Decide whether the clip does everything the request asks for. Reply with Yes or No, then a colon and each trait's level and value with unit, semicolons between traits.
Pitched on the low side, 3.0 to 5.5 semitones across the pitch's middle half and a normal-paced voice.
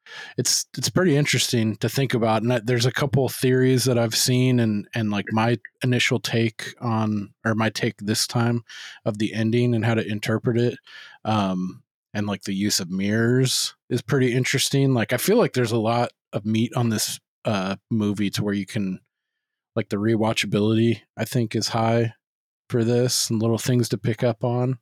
No: low, 115 Hz; narrow, 2.5 semitones; average, 195 wpm